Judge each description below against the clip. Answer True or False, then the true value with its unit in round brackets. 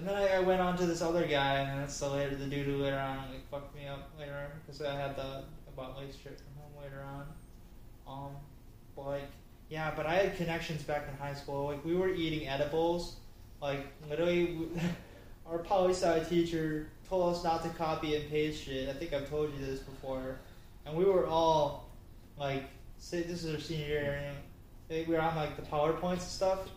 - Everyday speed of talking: False (210 wpm)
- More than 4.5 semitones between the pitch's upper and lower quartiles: False (3.1 semitones)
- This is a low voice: False (145 Hz)